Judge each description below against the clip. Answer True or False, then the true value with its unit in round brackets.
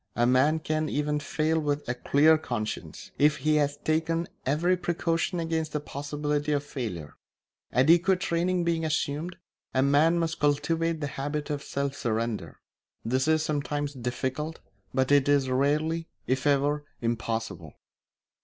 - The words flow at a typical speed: True (145 wpm)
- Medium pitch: True (145 Hz)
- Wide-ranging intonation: False (2.9 semitones)